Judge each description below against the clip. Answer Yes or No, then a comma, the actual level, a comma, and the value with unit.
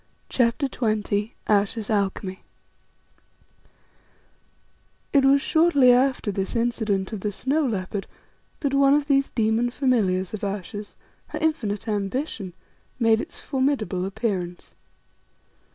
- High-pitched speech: Yes, high, 220 Hz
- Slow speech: Yes, slow, 110 wpm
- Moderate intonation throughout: Yes, average, 5.0 semitones